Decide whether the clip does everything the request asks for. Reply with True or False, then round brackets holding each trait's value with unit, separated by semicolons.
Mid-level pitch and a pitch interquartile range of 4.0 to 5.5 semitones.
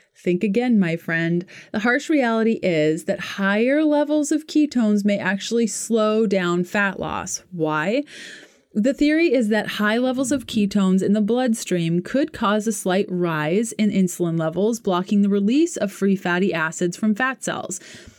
False (210 Hz; 4.7 semitones)